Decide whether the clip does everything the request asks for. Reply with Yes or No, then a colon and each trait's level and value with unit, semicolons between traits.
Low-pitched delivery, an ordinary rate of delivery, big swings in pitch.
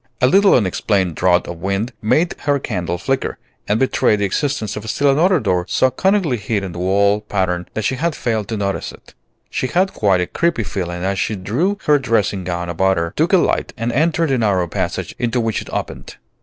No: low, 105 Hz; fast, 210 wpm; wide, 6.1 semitones